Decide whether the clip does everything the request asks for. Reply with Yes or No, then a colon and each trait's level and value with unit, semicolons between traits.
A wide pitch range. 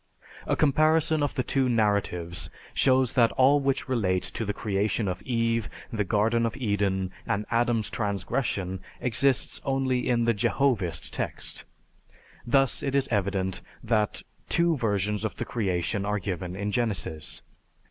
No: average, 4.4 semitones